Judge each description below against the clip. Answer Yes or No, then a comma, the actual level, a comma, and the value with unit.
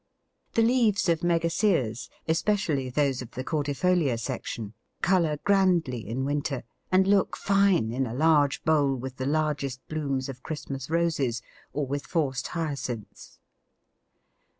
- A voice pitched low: No, medium, 145 Hz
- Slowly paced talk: Yes, slow, 130 wpm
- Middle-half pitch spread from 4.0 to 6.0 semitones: Yes, average, 4.4 semitones